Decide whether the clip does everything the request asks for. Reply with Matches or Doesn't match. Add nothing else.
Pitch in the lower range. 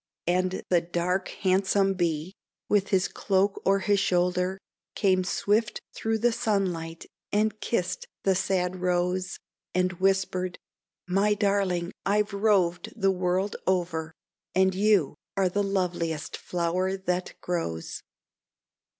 Doesn't match